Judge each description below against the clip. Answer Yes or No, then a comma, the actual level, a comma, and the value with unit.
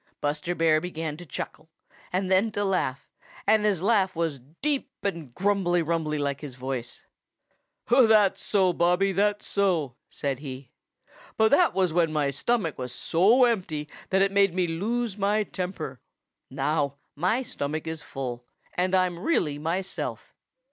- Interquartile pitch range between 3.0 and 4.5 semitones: No, average, 5.0 semitones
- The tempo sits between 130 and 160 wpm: Yes, average, 150 wpm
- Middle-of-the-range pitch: Yes, medium, 175 Hz